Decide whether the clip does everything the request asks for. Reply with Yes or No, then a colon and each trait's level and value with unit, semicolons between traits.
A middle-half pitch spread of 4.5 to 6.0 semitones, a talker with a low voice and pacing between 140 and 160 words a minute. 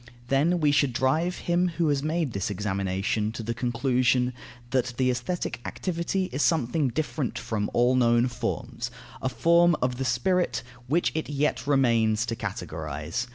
Yes: average, 4.9 semitones; low, 125 Hz; average, 155 wpm